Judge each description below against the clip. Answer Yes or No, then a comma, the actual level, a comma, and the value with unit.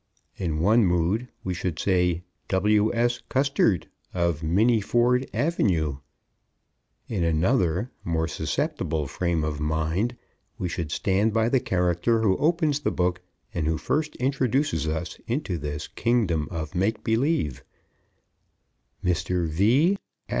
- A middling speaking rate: No, slow, 120 wpm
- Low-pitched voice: Yes, very low, 90 Hz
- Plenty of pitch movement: Yes, wide, 6.4 semitones